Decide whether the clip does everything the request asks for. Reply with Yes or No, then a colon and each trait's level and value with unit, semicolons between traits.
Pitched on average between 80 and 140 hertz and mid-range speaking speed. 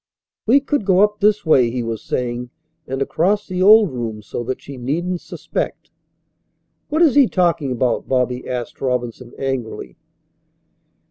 Yes: low, 135 Hz; average, 150 wpm